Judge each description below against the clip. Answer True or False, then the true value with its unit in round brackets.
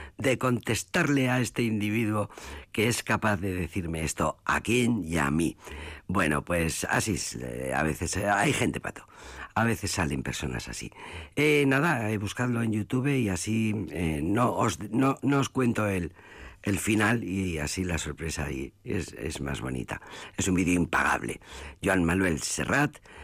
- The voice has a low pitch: True (100 Hz)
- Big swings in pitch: True (6.3 semitones)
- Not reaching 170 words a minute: False (175 wpm)